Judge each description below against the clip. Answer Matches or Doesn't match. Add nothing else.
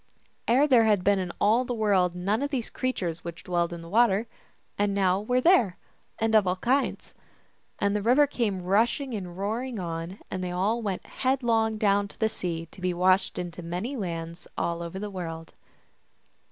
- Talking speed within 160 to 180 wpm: Doesn't match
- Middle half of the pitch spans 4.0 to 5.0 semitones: Matches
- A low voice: Doesn't match